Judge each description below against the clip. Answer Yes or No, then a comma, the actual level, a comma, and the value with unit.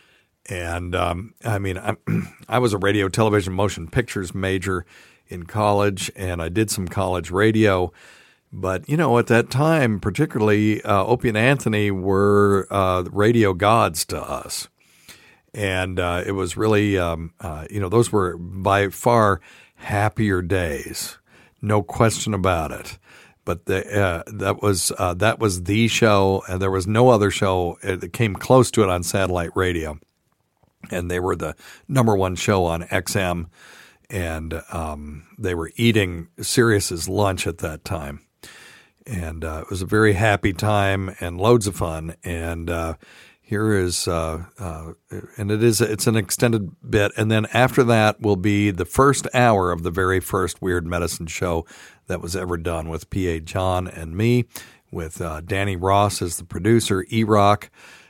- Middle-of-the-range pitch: No, very low, 95 Hz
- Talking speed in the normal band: Yes, average, 165 wpm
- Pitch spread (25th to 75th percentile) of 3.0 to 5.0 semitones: Yes, average, 3.4 semitones